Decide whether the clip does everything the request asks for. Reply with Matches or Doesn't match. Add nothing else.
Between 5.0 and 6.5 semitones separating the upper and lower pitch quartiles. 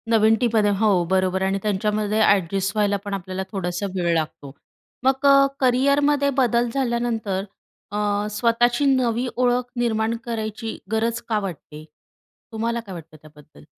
Doesn't match